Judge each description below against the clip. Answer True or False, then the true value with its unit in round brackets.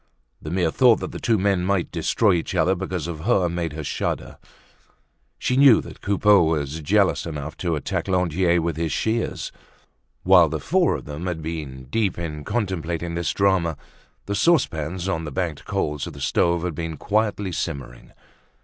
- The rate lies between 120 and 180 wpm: True (175 wpm)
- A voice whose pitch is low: True (85 Hz)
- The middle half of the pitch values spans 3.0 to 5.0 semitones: True (3.6 semitones)